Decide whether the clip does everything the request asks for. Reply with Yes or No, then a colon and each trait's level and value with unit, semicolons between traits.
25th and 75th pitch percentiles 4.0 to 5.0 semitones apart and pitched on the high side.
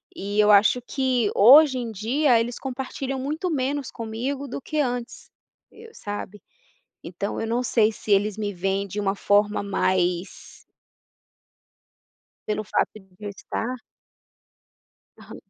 Yes: average, 4.4 semitones; high, 225 Hz